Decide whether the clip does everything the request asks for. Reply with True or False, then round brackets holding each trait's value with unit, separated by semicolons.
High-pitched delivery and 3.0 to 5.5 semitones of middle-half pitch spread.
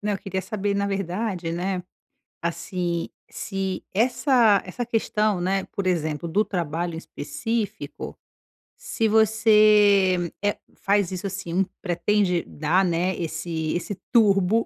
True (195 Hz; 3.4 semitones)